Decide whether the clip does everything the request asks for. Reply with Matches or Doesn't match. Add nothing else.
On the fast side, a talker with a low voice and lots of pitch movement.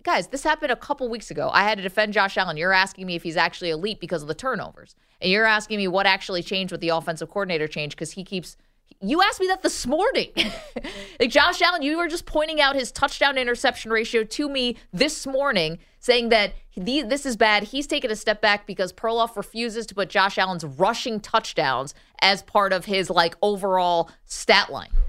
Doesn't match